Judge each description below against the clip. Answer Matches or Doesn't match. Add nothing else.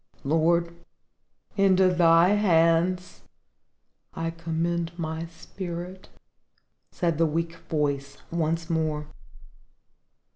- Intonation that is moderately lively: Doesn't match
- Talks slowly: Matches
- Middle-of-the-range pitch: Matches